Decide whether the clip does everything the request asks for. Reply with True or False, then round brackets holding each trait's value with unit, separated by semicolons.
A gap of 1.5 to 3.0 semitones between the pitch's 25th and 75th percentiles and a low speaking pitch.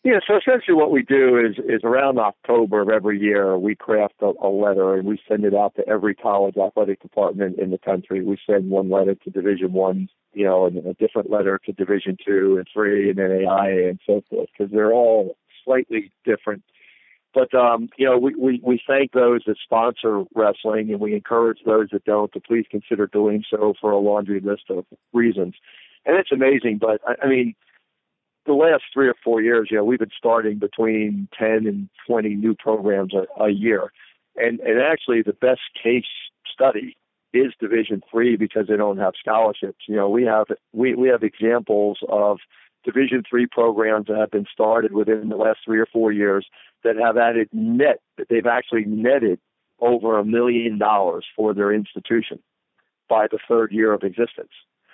True (2.4 semitones; 110 Hz)